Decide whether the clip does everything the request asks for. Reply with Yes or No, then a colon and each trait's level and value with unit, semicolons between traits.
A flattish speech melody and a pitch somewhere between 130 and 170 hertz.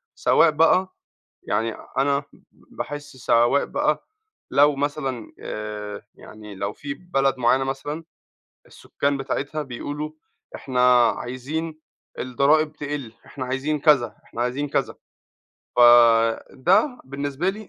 No: average, 3.6 semitones; low, 135 Hz